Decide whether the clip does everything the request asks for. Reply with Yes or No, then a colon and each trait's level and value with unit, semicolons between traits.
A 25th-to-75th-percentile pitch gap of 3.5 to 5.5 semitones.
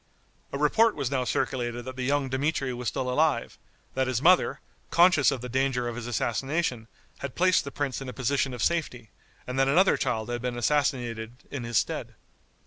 No: average, 2.9 semitones